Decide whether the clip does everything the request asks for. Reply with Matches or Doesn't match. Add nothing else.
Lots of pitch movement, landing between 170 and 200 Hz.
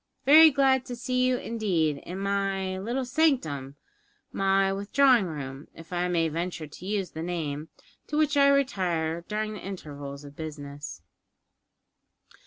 Matches